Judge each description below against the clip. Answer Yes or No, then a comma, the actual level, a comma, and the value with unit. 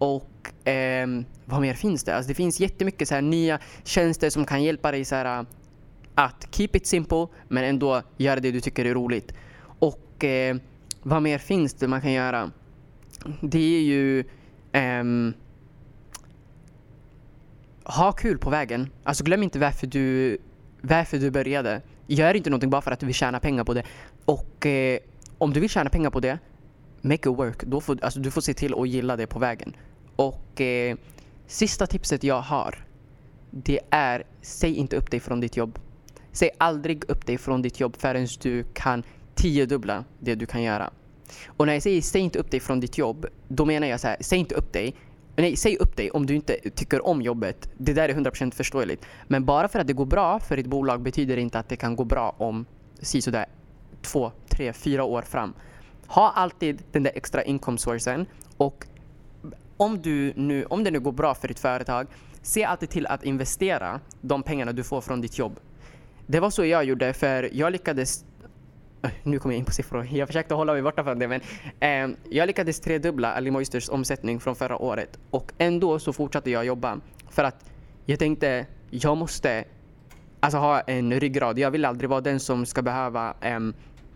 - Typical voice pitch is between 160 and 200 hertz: No, low, 135 Hz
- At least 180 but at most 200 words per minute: Yes, average, 190 wpm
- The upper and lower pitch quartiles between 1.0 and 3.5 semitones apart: Yes, average, 2.9 semitones